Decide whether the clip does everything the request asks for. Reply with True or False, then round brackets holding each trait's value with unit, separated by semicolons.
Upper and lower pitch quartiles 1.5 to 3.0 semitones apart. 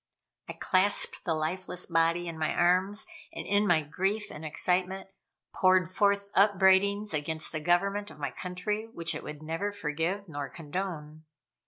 False (3.8 semitones)